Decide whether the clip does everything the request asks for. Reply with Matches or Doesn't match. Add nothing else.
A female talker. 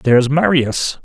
Doesn't match